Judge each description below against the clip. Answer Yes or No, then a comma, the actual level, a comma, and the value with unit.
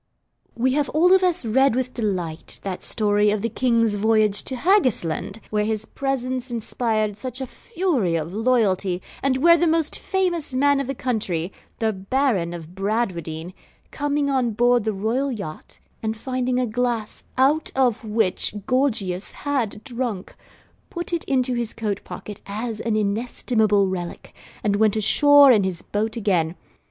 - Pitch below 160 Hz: No, high, 230 Hz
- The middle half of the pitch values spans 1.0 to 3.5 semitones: No, average, 4.3 semitones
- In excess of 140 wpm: Yes, average, 155 wpm